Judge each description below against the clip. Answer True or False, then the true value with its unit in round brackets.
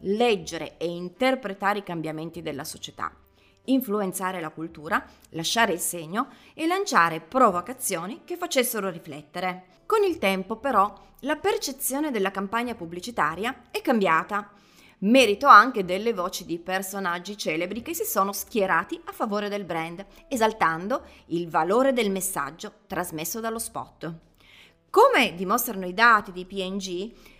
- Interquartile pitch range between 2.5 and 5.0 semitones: False (5.6 semitones)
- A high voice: True (200 Hz)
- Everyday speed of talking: True (130 wpm)